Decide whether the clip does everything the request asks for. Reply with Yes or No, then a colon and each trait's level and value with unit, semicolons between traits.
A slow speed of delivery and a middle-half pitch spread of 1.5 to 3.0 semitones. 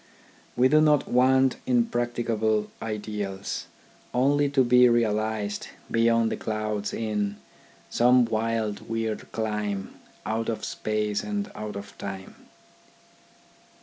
Yes: slow, 115 wpm; average, 2.7 semitones